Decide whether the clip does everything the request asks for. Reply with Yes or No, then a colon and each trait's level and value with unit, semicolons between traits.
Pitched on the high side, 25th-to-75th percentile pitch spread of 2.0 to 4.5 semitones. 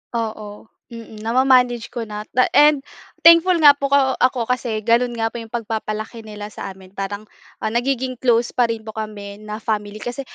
Yes: high, 230 Hz; average, 2.8 semitones